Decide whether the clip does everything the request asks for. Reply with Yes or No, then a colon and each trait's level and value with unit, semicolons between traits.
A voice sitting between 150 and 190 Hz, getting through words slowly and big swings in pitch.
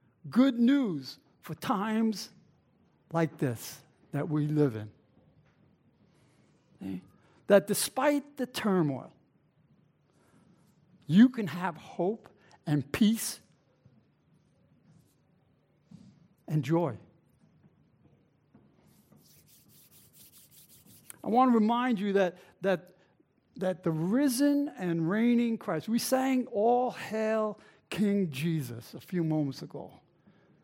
Yes: medium, 185 Hz; slow, 90 wpm; wide, 6.3 semitones